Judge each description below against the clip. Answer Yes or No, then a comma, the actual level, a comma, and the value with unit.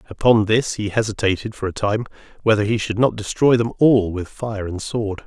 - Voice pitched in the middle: No, low, 105 Hz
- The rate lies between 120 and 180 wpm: No, fast, 205 wpm